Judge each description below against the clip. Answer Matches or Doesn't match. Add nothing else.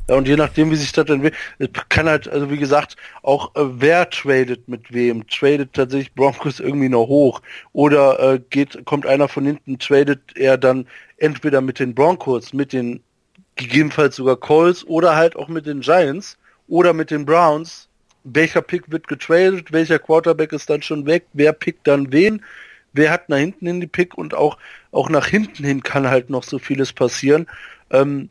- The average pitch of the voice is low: Doesn't match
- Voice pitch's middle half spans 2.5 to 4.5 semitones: Matches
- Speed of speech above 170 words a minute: Matches